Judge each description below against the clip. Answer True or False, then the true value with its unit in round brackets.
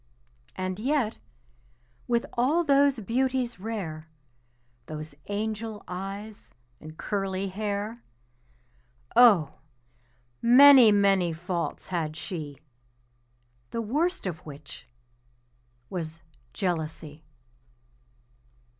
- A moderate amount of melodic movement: False (5.9 semitones)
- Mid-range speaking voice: False (200 Hz)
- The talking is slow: True (80 wpm)